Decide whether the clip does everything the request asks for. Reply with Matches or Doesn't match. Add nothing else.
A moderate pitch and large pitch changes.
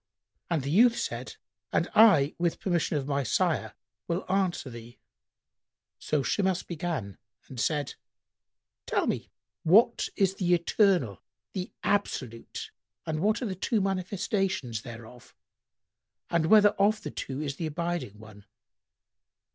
Matches